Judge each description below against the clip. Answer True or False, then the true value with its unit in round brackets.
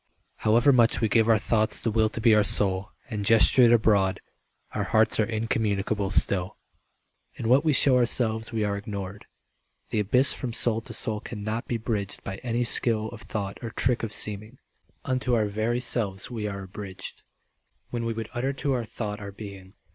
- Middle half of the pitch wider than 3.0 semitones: False (2.4 semitones)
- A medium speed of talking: True (190 wpm)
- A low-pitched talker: True (110 Hz)